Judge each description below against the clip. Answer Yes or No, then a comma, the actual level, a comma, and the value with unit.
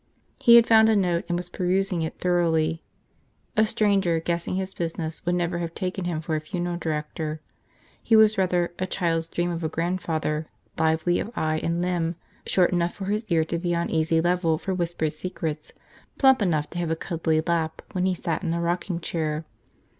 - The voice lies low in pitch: No, medium, 170 Hz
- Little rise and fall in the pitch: Yes, narrow, 2.1 semitones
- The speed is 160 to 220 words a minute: Yes, average, 195 wpm